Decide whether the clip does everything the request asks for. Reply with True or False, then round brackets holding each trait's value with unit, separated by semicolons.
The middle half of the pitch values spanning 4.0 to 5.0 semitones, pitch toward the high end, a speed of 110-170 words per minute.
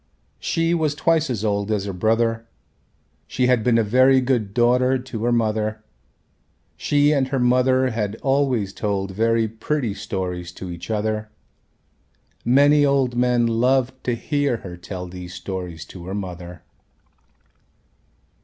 False (4.4 semitones; 115 Hz; 145 wpm)